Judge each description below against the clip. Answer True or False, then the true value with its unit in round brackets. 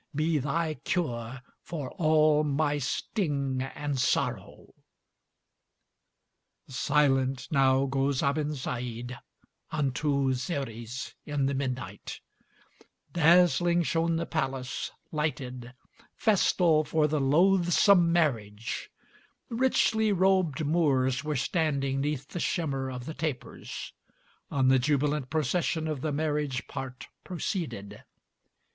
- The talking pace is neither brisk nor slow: False (100 wpm)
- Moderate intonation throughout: True (3.5 semitones)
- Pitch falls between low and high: True (145 Hz)